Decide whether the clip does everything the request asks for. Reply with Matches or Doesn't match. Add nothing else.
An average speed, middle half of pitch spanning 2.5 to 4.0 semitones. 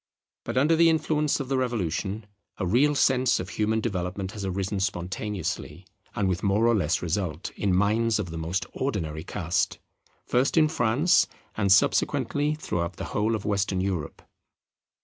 Doesn't match